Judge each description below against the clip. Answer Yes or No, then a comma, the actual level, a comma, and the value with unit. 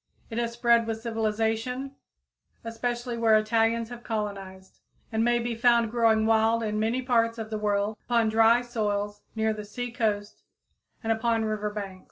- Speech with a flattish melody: Yes, narrow, 1.6 semitones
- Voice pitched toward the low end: No, high, 225 Hz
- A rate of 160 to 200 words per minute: Yes, average, 165 wpm